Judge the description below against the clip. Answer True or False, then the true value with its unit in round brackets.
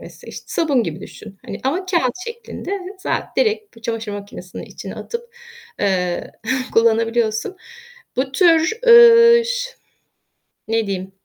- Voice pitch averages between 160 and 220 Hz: False (260 Hz)